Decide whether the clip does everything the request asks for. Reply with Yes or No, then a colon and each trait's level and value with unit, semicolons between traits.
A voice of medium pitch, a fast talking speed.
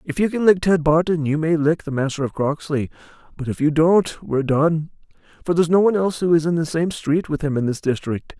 Yes: medium, 160 Hz; fast, 250 wpm